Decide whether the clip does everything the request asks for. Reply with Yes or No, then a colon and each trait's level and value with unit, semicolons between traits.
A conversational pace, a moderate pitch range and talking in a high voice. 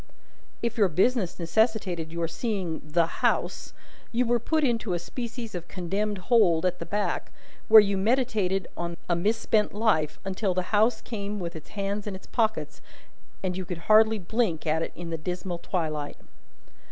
Yes: average, 170 wpm; average, 4.3 semitones; high, 195 Hz